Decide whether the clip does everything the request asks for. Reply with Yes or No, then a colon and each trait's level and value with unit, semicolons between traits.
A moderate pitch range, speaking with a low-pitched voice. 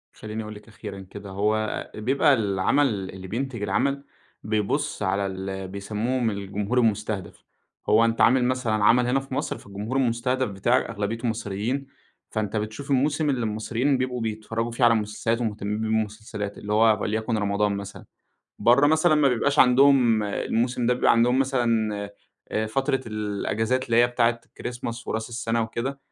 Yes: average, 3.1 semitones; low, 115 Hz